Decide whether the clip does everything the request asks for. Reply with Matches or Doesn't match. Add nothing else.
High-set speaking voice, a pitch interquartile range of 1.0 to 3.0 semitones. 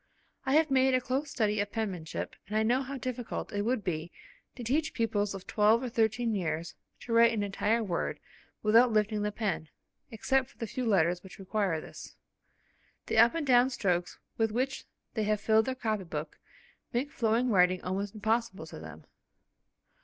Doesn't match